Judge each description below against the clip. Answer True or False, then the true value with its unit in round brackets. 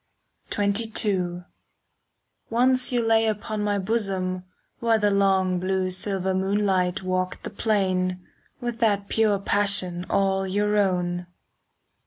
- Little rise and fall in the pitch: True (2.3 semitones)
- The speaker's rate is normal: False (115 wpm)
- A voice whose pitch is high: True (195 Hz)